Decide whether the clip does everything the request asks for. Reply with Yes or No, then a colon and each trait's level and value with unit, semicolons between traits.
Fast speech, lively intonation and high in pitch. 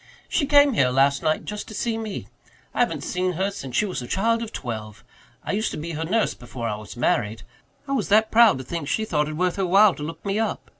No: fast, 255 wpm; wide, 8.1 semitones; medium, 180 Hz